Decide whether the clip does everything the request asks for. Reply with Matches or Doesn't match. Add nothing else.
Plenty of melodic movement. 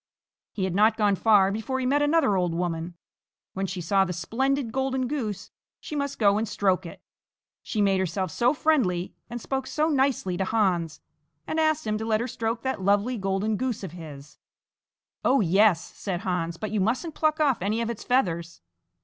Matches